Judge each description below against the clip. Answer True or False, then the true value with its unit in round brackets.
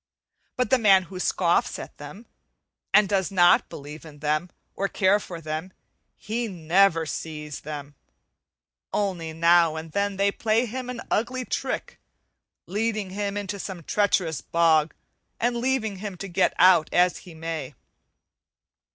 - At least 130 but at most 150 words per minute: True (145 wpm)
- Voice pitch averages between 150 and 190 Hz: True (185 Hz)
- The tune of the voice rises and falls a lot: False (4.3 semitones)